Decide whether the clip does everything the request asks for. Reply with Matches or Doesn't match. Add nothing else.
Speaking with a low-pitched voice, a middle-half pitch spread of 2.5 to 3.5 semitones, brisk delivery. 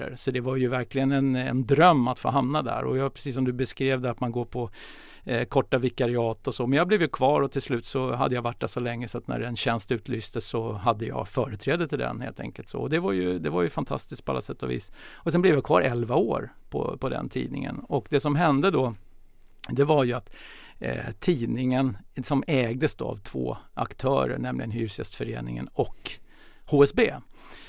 Matches